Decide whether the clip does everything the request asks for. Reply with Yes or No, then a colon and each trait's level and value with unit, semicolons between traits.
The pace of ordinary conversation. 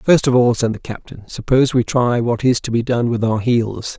No: fast, 255 wpm